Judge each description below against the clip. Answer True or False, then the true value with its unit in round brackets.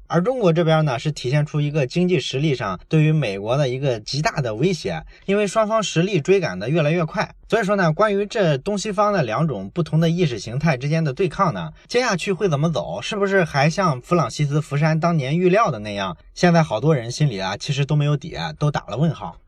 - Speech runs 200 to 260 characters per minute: False (350 characters per minute)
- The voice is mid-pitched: True (160 Hz)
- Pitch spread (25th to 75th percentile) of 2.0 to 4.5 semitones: True (3.8 semitones)